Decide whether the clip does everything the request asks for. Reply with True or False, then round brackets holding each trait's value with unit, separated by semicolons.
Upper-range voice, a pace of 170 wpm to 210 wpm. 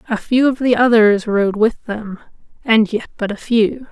True (225 Hz; 200 wpm)